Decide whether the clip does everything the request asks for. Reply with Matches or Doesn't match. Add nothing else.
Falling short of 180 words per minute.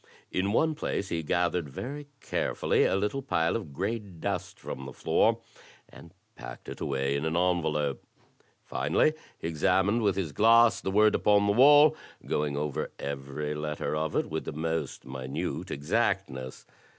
Matches